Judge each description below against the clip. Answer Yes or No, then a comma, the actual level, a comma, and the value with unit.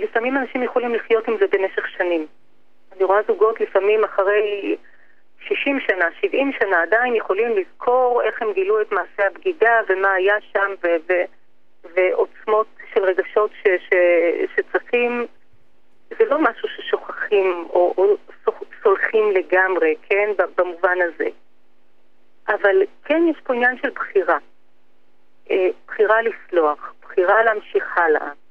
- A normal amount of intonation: No, wide, 8.5 semitones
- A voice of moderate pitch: No, high, 215 Hz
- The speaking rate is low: No, average, 130 wpm